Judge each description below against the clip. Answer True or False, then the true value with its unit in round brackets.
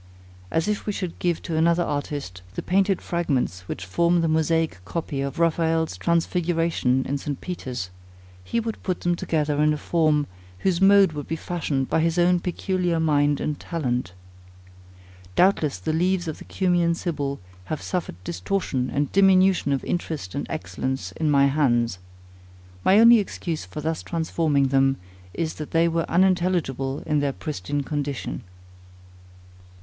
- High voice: False (160 Hz)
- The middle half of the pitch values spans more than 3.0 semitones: True (3.9 semitones)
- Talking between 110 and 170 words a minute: True (155 wpm)